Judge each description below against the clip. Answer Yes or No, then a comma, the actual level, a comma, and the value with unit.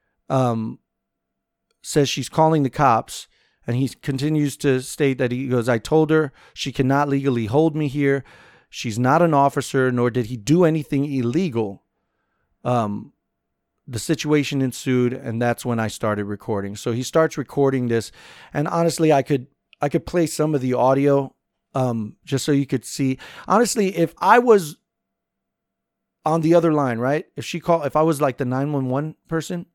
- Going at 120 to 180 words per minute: Yes, average, 170 wpm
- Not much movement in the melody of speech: No, average, 3.7 semitones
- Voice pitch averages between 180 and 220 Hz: No, medium, 140 Hz